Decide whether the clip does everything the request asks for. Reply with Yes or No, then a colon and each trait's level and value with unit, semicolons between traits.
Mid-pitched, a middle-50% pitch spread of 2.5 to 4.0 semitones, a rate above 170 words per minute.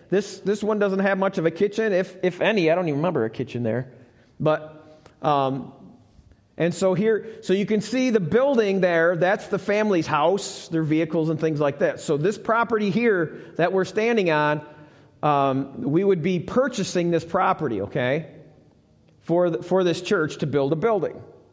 No: medium, 180 Hz; average, 4.9 semitones; average, 185 wpm